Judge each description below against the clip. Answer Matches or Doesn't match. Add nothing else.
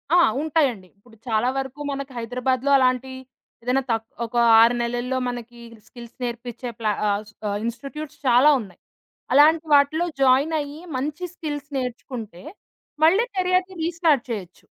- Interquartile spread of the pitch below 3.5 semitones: Doesn't match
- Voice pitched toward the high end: Matches